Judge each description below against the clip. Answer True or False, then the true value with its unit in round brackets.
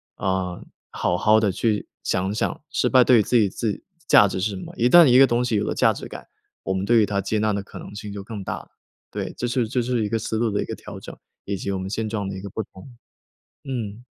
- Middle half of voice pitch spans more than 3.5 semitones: False (3.2 semitones)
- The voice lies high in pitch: False (105 Hz)